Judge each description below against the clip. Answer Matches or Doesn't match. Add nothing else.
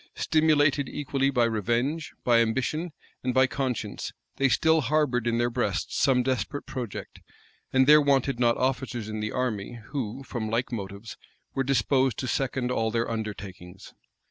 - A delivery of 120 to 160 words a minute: Matches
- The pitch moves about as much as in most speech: Matches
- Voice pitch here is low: Matches